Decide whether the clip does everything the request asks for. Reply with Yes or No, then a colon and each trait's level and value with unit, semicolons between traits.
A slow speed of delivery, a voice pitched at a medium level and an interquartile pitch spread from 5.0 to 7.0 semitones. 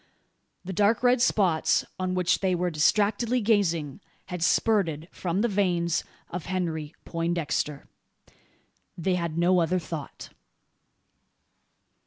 No: slow, 115 wpm; medium, 180 Hz; average, 3.4 semitones